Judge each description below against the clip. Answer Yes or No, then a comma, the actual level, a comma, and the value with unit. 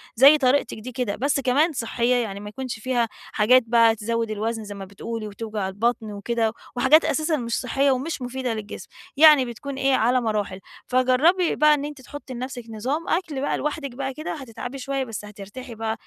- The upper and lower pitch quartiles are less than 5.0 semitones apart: Yes, average, 3.6 semitones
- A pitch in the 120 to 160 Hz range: No, very high, 250 Hz